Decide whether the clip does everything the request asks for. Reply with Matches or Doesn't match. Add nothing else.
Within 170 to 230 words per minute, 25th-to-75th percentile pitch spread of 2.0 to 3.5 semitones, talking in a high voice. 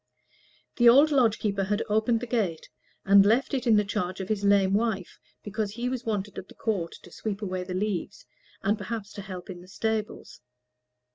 Matches